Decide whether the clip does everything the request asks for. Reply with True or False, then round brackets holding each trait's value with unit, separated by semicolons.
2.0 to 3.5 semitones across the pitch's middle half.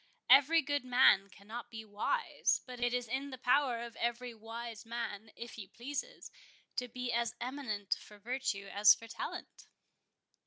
True (2.5 semitones)